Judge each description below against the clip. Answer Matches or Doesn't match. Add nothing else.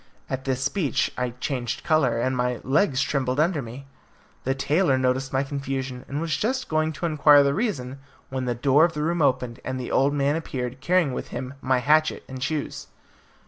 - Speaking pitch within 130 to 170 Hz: Matches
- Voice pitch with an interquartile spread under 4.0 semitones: Matches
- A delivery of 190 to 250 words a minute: Matches